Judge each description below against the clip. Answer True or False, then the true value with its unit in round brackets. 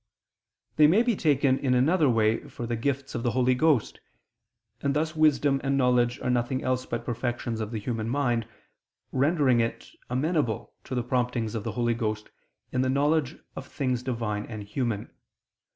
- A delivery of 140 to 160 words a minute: False (175 wpm)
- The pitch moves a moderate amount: True (3.0 semitones)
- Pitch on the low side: True (125 Hz)